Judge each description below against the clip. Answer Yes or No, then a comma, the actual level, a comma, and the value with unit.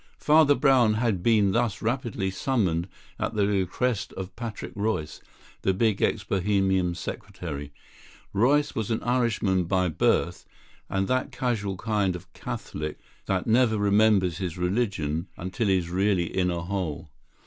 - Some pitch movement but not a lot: Yes, average, 3.7 semitones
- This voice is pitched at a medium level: No, low, 100 Hz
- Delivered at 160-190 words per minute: No, average, 145 wpm